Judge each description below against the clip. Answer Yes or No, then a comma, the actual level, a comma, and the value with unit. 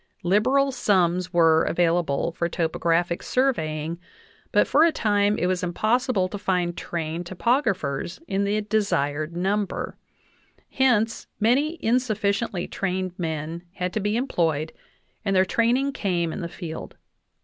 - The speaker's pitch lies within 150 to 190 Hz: Yes, medium, 185 Hz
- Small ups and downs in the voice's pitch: No, average, 4.3 semitones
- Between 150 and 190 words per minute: No, average, 140 wpm